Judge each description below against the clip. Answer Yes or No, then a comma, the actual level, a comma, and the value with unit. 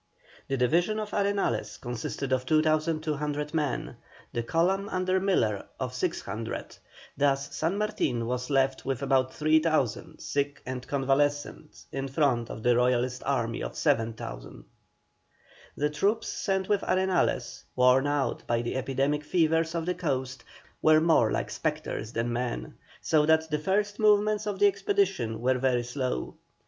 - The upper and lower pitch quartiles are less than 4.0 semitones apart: No, average, 5.1 semitones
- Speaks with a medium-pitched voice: Yes, medium, 145 Hz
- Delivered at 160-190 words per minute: No, average, 145 wpm